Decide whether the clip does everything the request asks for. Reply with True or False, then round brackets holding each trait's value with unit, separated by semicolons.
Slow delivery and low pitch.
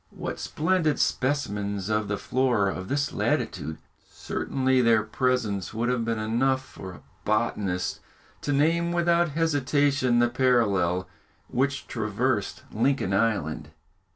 True (125 wpm; 120 Hz)